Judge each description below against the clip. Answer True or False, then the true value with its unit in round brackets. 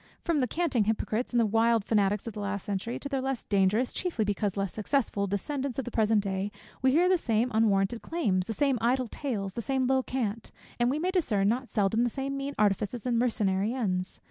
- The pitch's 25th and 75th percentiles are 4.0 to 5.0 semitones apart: True (4.5 semitones)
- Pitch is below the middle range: False (230 Hz)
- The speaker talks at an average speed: False (215 wpm)